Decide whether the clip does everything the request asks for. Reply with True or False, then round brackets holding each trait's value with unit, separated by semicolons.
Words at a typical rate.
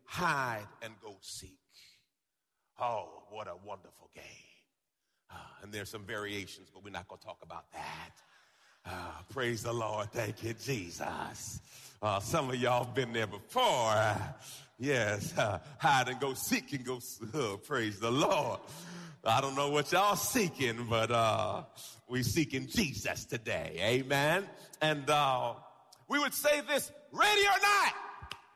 True (150 wpm)